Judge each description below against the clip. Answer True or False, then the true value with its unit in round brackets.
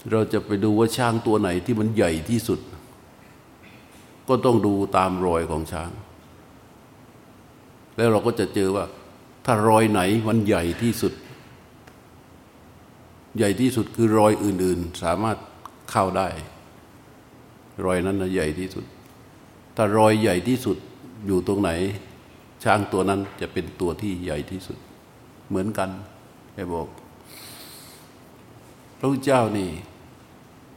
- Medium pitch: False (100 Hz)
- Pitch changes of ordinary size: True (3.5 semitones)